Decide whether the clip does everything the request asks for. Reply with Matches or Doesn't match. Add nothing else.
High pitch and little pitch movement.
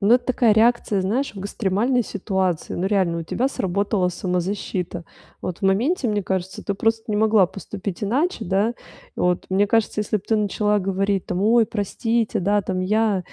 Doesn't match